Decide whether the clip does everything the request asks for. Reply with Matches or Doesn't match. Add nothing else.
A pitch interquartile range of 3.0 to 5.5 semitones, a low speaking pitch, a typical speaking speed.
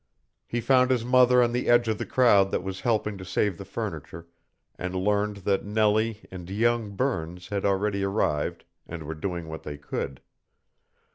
Matches